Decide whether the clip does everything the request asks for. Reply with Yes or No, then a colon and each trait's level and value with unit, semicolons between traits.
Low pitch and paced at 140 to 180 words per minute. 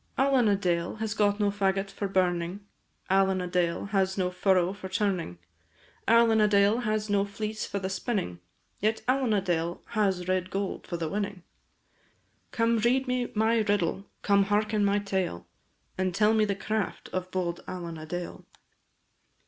No: high, 200 Hz; average, 165 wpm